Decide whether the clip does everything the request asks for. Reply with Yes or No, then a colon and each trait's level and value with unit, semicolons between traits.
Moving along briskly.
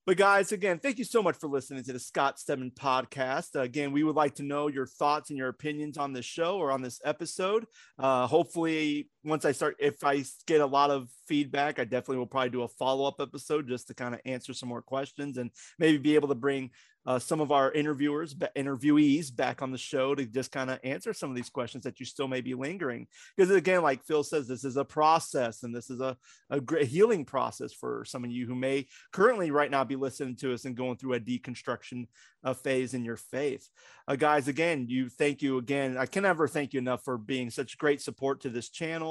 Yes: fast, 235 wpm